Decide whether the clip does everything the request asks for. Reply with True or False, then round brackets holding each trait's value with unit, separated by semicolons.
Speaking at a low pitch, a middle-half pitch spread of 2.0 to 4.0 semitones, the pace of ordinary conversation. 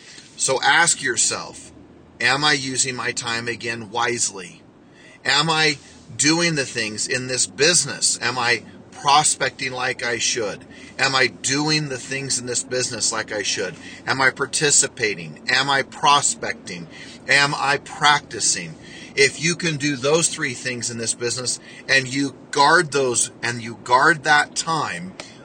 True (130 Hz; 3.6 semitones; 150 wpm)